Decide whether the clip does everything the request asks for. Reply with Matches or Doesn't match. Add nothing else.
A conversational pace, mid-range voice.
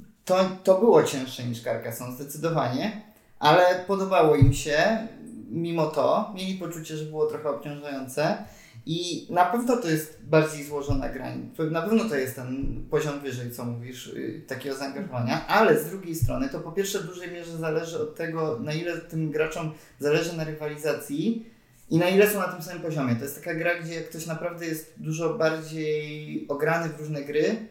Doesn't match